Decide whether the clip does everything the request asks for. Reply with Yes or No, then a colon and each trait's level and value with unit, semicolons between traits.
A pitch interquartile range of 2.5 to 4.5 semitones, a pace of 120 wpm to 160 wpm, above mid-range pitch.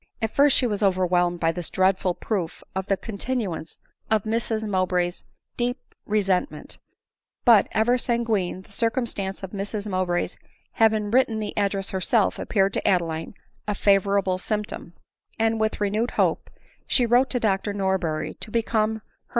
Yes: average, 3.1 semitones; average, 150 wpm; high, 205 Hz